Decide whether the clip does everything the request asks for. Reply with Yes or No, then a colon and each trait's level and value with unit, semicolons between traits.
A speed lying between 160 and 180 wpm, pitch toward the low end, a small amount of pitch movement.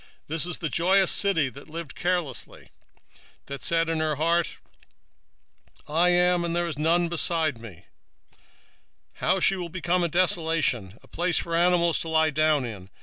No: average, 165 wpm; medium, 165 Hz; narrow, 2.3 semitones